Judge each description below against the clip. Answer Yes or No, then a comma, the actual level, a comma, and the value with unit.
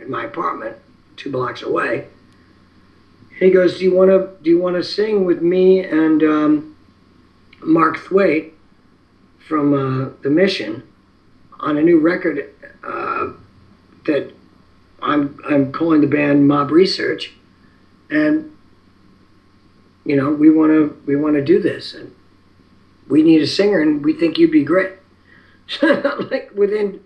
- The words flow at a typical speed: Yes, average, 145 wpm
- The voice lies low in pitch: No, medium, 155 Hz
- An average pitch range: No, wide, 7.2 semitones